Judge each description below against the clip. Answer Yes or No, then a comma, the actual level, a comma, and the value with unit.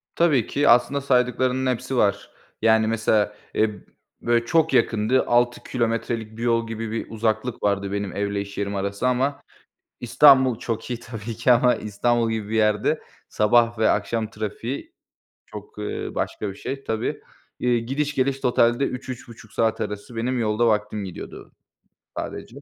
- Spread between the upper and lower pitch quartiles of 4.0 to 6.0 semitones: No, average, 2.7 semitones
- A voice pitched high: No, low, 115 Hz